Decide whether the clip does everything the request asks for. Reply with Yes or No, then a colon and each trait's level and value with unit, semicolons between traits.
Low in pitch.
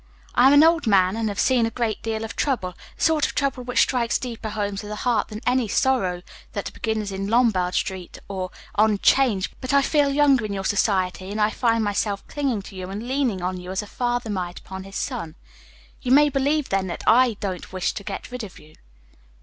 No: high, 220 Hz